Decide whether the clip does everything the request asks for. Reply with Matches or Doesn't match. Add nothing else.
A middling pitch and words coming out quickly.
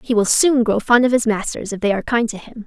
Doesn't match